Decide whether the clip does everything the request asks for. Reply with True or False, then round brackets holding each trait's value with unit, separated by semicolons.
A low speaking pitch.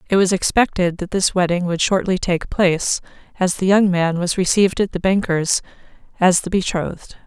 False (185 Hz)